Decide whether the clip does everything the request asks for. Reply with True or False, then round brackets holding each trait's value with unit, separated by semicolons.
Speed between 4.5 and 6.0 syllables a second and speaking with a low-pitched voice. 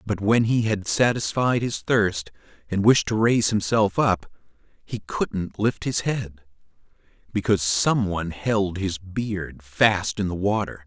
False (4.0 syllables/s; 100 Hz)